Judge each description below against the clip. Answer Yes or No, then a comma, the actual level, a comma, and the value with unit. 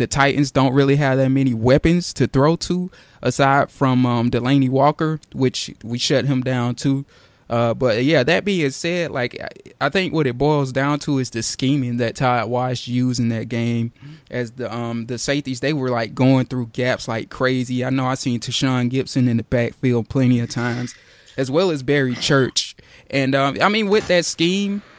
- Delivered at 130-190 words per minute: No, average, 200 wpm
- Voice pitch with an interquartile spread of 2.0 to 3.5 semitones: Yes, narrow, 2.6 semitones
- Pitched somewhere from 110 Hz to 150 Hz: Yes, low, 130 Hz